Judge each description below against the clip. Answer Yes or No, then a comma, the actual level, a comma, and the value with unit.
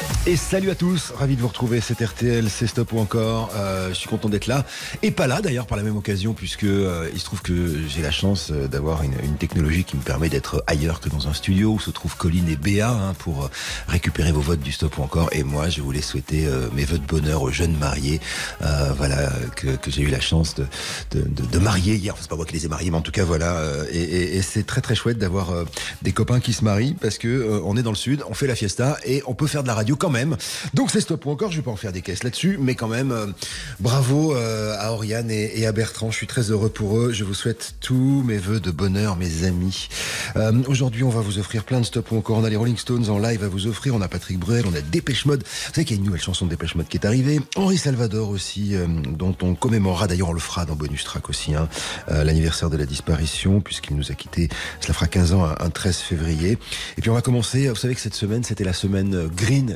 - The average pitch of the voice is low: Yes, low, 100 Hz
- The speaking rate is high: Yes, fast, 275 wpm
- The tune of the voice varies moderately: No, wide, 6.1 semitones